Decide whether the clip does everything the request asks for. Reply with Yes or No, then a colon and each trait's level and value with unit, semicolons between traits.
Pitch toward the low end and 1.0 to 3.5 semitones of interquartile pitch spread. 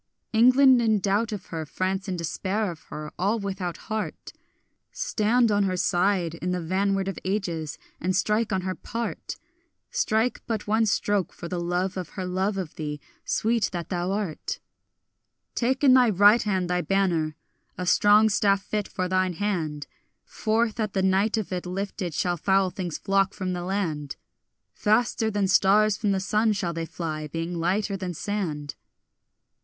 No: high, 195 Hz; average, 3.0 semitones